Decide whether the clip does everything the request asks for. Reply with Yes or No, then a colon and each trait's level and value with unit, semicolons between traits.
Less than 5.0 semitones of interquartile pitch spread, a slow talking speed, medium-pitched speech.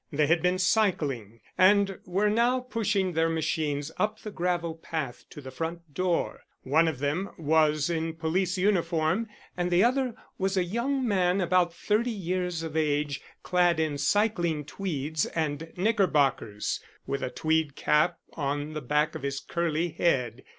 No: average, 3.9 semitones; average, 155 wpm; medium, 165 Hz